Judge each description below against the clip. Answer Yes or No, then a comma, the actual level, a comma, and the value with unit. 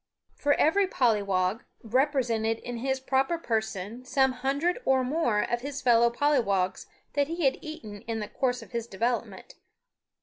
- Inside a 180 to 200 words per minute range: No, average, 155 wpm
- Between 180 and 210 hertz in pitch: No, very high, 250 Hz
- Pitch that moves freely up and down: No, average, 3.8 semitones